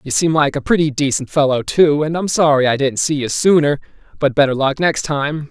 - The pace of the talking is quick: Yes, fast, 230 wpm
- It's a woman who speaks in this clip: No, male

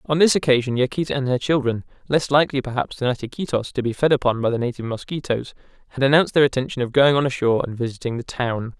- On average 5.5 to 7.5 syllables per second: Yes, 7.0 syllables/s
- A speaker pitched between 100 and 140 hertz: Yes, low, 130 Hz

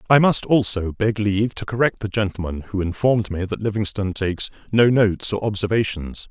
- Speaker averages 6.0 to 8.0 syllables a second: No, 5.8 syllables/s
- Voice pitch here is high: No, low, 105 Hz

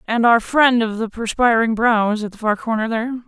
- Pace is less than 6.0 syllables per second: Yes, 5.7 syllables/s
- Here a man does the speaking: No, female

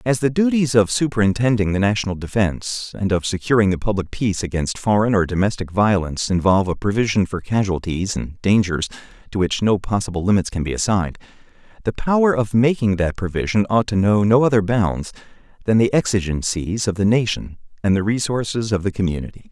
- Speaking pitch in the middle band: No, low, 105 Hz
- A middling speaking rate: Yes, average, 180 wpm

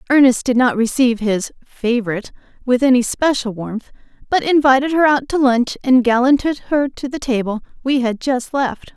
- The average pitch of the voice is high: Yes, very high, 255 Hz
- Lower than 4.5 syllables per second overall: No, 5.1 syllables/s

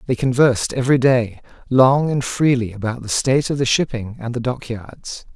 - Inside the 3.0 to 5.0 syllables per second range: No, 5.2 syllables/s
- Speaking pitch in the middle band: No, low, 125 Hz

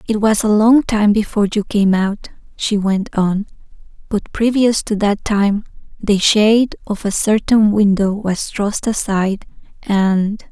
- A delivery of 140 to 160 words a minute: Yes, average, 155 wpm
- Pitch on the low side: No, high, 210 Hz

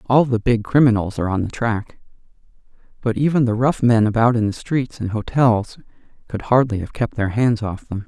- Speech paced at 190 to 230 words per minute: Yes, average, 200 wpm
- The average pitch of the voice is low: Yes, low, 115 Hz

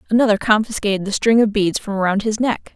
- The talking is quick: Yes, fast, 220 wpm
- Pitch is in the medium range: No, high, 210 Hz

